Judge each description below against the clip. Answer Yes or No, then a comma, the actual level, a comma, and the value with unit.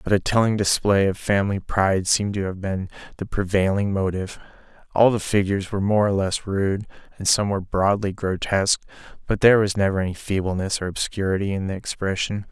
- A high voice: No, low, 100 Hz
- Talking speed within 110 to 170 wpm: No, average, 180 wpm